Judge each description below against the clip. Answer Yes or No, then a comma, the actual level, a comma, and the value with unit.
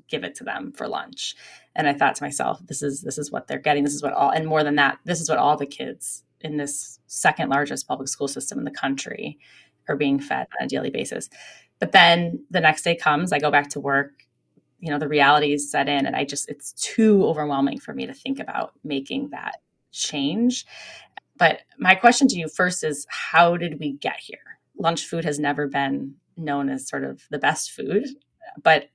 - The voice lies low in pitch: No, medium, 150 Hz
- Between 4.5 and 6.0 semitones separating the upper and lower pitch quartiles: No, average, 3.2 semitones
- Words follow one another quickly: Yes, fast, 220 wpm